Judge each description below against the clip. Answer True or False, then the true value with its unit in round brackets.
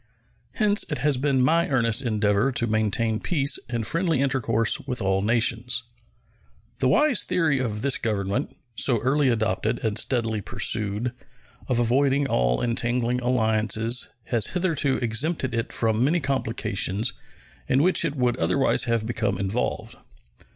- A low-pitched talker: True (120 Hz)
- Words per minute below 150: True (140 wpm)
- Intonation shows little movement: False (3.8 semitones)